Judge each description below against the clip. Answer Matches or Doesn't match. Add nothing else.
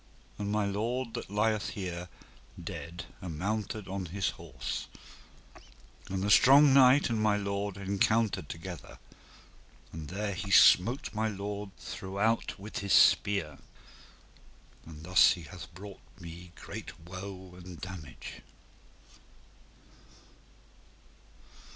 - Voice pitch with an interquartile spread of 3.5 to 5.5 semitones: Doesn't match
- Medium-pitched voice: Doesn't match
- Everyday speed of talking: Doesn't match